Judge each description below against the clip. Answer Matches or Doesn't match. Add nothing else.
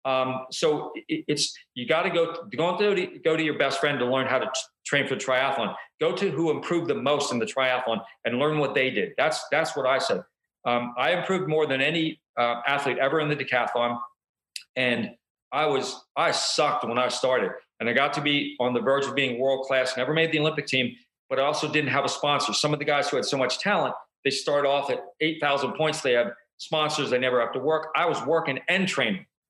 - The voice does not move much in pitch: Doesn't match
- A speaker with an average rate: Doesn't match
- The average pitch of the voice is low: Doesn't match